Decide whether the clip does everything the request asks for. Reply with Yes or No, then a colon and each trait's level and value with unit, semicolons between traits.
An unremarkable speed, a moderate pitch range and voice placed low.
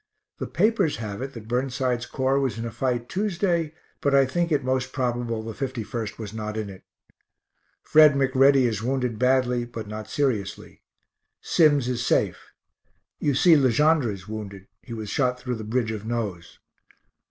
Yes: average, 170 wpm; average, 3.7 semitones; low, 125 Hz